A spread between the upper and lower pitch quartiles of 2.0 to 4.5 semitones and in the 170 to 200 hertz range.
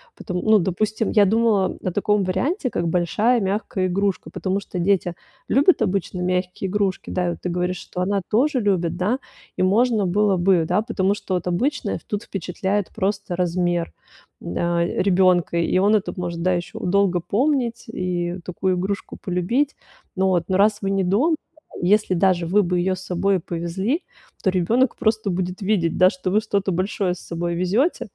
Yes: narrow, 2.6 semitones; high, 190 Hz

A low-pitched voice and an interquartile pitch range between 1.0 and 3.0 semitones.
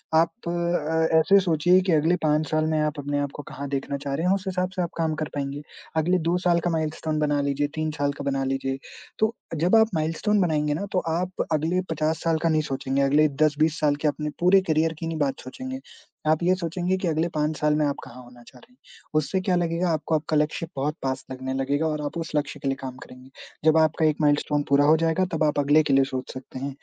No: medium, 155 Hz; narrow, 2.6 semitones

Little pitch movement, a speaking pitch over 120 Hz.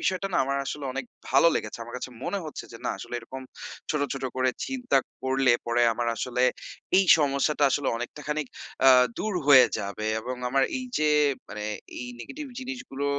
No: average, 3.5 semitones; low, 135 Hz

